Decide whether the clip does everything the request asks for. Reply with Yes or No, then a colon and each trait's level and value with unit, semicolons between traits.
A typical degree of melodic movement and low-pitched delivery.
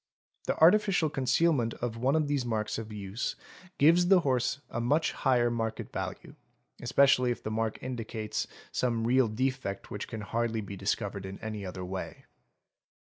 Yes: average, 3.6 semitones; low, 120 Hz